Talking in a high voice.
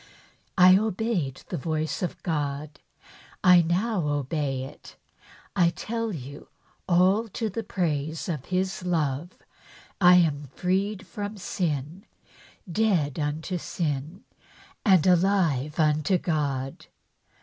No: medium, 170 Hz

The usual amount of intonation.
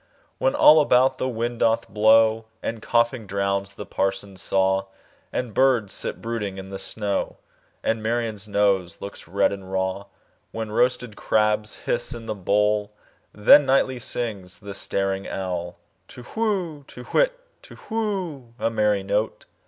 Yes: average, 3.5 semitones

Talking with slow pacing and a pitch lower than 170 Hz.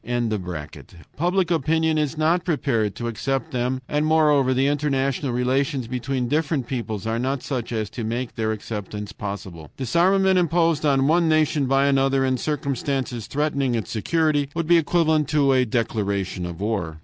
No: average, 160 wpm; low, 135 Hz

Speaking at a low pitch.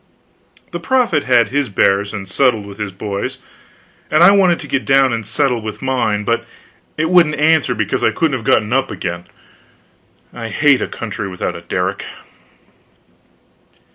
Yes: low, 120 Hz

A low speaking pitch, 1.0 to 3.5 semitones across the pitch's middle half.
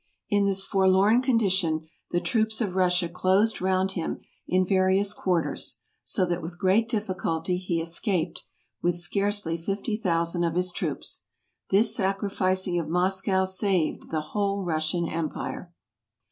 No: medium, 185 Hz; narrow, 2.4 semitones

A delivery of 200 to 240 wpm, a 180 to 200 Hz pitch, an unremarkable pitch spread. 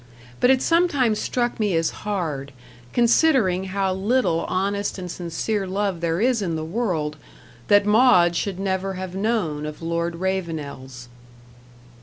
No: average, 140 wpm; high, 190 Hz; average, 4.2 semitones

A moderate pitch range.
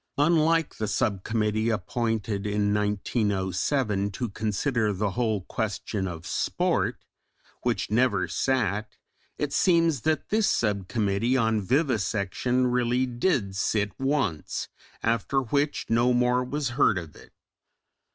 Yes: average, 4.0 semitones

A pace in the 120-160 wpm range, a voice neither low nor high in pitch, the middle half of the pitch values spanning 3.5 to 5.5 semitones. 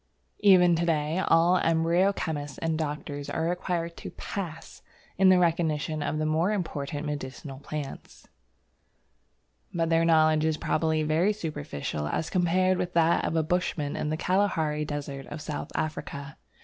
No: average, 150 wpm; medium, 160 Hz; narrow, 2.5 semitones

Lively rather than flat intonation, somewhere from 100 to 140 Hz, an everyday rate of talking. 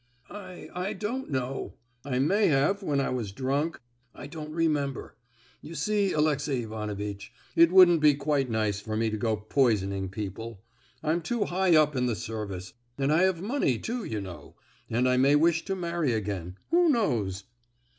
Yes: wide, 7.4 semitones; low, 135 Hz; average, 160 wpm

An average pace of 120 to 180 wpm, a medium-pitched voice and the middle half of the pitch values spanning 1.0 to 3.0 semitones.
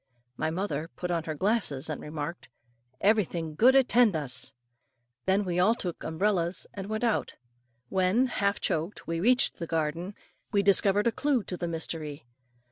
No: average, 165 wpm; medium, 180 Hz; average, 4.5 semitones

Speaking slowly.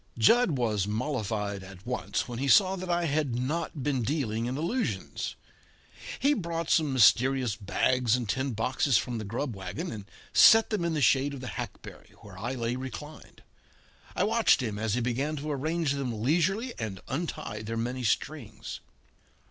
No: average, 170 wpm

